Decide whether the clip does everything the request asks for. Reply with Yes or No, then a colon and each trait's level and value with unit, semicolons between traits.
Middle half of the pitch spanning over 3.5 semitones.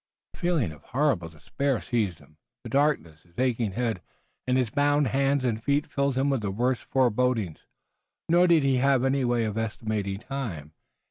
Yes: average, 4.7 semitones